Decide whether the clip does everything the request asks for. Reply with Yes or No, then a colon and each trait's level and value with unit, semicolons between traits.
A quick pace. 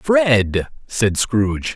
No: slow, 100 wpm